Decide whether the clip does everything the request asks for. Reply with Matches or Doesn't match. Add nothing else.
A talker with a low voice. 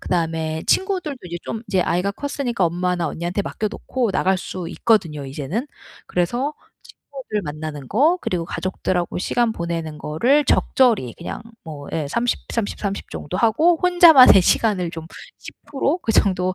Doesn't match